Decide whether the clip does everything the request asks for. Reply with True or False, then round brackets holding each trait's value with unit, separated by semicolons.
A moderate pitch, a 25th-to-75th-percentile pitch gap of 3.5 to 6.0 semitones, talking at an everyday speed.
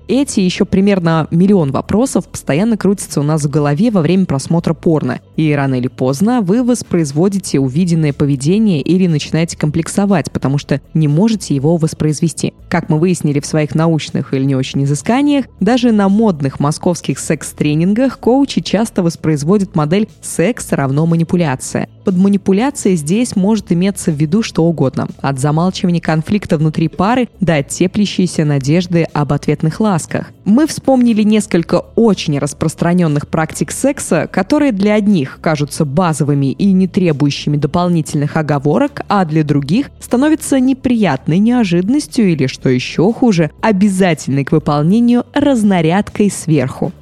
True (175 Hz; 5.2 semitones; 135 wpm)